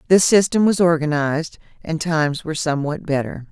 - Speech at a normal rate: Yes, average, 155 wpm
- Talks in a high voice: No, medium, 160 Hz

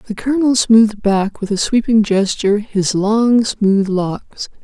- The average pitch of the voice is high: Yes, high, 215 Hz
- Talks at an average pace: Yes, average, 155 wpm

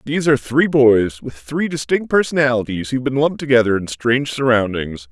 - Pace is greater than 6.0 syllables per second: No, 5.8 syllables/s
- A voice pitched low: Yes, low, 130 Hz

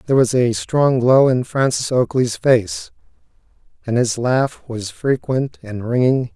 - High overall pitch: No, low, 125 Hz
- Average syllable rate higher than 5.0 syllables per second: No, 4.0 syllables/s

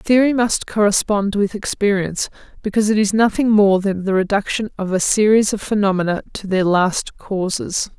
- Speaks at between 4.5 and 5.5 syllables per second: Yes, 5.1 syllables/s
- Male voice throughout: No, female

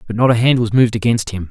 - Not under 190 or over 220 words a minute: No, fast, 320 wpm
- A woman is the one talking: No, male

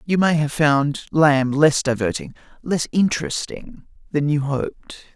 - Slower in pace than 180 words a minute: Yes, average, 140 wpm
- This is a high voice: No, medium, 150 Hz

